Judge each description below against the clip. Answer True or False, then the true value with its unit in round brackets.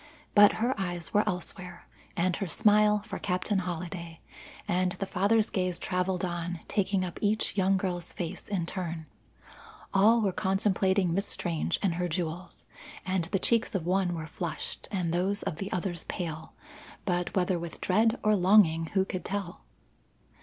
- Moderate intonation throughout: False (2.3 semitones)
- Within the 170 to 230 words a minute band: False (160 wpm)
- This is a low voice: False (185 Hz)